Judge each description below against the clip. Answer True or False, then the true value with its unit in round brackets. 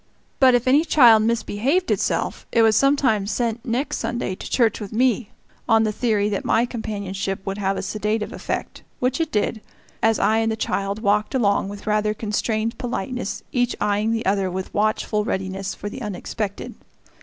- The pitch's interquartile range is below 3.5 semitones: True (2.8 semitones)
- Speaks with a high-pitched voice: True (215 Hz)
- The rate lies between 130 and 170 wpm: False (180 wpm)